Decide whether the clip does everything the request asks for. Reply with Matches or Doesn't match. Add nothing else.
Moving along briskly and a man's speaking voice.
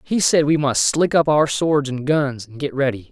Matches